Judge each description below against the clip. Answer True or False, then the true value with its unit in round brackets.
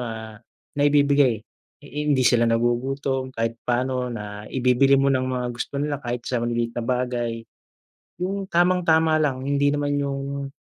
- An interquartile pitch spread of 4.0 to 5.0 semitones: False (3.1 semitones)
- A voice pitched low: True (130 Hz)